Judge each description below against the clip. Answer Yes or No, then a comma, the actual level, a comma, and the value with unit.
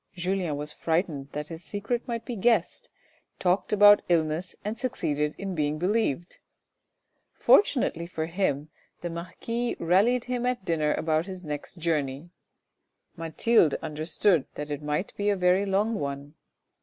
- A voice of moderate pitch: Yes, medium, 175 Hz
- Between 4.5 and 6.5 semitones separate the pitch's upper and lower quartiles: Yes, average, 5.1 semitones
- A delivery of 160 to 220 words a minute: No, average, 145 wpm